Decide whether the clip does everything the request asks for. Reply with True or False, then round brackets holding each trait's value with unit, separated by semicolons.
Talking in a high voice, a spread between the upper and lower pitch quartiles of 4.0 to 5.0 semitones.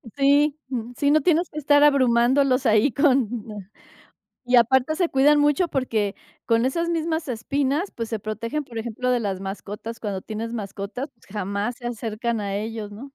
True (245 Hz; 4.7 semitones)